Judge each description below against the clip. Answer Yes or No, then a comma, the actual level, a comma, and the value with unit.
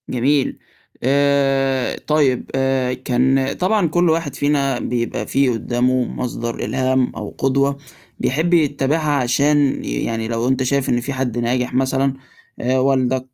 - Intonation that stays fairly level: Yes, narrow, 2.0 semitones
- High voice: No, low, 135 Hz